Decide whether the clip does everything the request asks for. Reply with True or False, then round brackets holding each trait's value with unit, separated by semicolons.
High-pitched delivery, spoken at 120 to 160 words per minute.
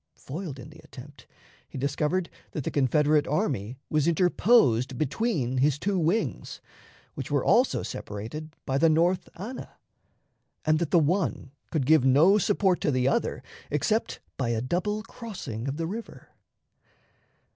False (155 Hz; 145 wpm)